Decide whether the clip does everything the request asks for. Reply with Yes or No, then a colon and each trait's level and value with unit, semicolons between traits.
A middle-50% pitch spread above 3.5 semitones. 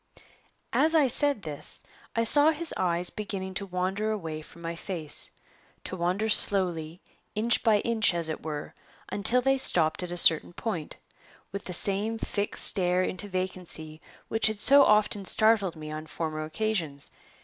Yes: average, 4.6 semitones